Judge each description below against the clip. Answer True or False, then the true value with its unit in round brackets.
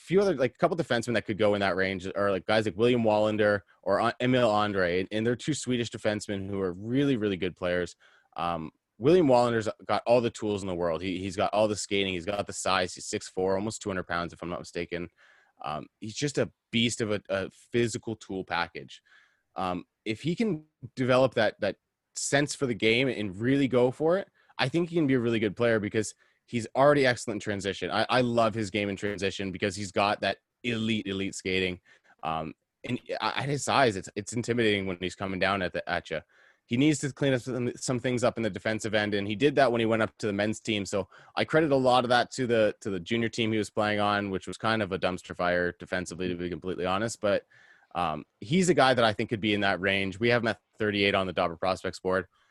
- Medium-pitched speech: False (105 Hz)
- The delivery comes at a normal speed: False (240 wpm)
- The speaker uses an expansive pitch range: False (3.8 semitones)